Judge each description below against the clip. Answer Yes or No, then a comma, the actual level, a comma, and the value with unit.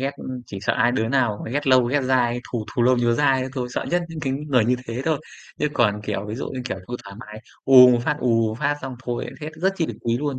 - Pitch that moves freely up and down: No, average, 3.0 semitones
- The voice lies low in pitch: Yes, low, 125 Hz